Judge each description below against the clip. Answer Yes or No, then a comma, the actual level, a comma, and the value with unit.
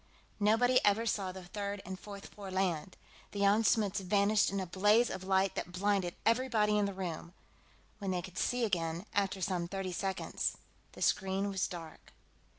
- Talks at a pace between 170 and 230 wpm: Yes, average, 175 wpm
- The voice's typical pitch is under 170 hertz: No, high, 195 Hz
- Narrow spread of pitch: Yes, narrow, 2.0 semitones